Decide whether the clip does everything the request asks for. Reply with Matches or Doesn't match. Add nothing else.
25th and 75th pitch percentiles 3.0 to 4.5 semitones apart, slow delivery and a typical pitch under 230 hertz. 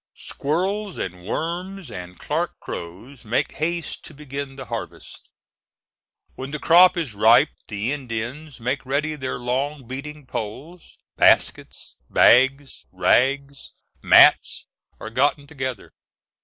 Matches